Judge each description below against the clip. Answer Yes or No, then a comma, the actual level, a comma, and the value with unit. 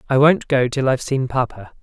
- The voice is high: No, low, 135 Hz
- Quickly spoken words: Yes, fast, 230 wpm